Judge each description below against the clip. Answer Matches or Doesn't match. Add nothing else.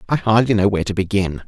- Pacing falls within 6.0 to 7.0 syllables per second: Matches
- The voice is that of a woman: Doesn't match